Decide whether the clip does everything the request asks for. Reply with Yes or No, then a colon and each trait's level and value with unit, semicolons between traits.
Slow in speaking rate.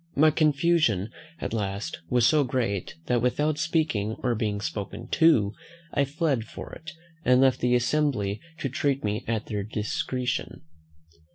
No: average, 150 wpm